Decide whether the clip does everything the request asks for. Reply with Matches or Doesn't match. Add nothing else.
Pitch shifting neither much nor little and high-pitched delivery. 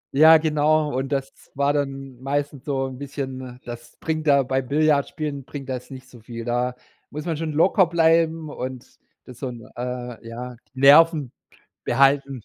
Doesn't match